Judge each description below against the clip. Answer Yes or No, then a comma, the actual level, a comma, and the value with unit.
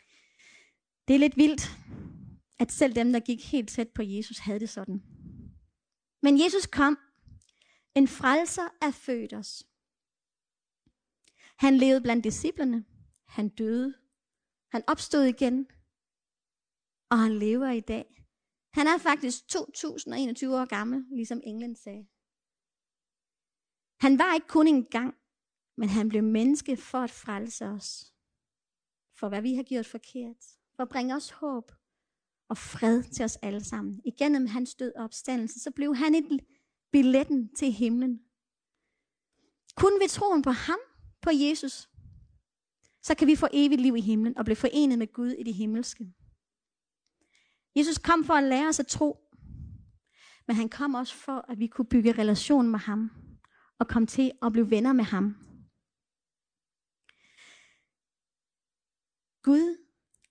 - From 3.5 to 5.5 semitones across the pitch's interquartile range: Yes, average, 3.8 semitones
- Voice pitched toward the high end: Yes, very high, 255 Hz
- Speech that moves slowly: Yes, slow, 140 wpm